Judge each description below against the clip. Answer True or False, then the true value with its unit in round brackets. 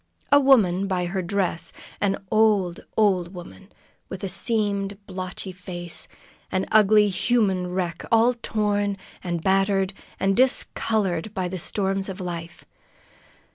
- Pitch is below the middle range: False (195 Hz)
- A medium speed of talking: False (130 wpm)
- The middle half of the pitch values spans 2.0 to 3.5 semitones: True (2.4 semitones)